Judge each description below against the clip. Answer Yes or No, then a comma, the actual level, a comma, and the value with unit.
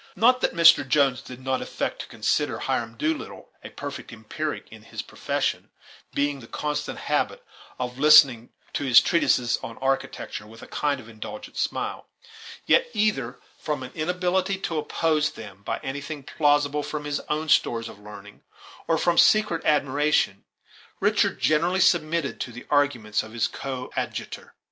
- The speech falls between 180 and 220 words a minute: No, average, 160 wpm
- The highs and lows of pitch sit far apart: No, average, 4.4 semitones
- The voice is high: No, medium, 145 Hz